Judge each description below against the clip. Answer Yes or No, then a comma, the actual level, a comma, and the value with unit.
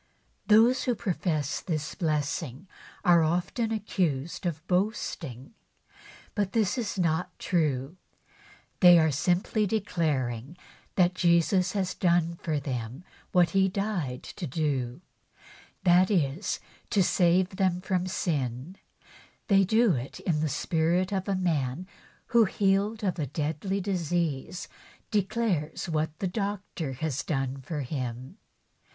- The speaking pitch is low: No, medium, 175 Hz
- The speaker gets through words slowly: Yes, slow, 130 wpm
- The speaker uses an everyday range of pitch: Yes, average, 4.4 semitones